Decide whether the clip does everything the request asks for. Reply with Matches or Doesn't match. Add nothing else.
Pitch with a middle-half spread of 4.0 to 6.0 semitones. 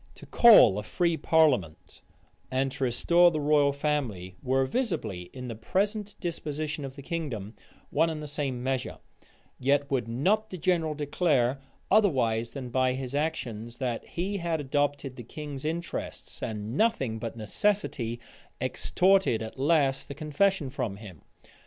Matches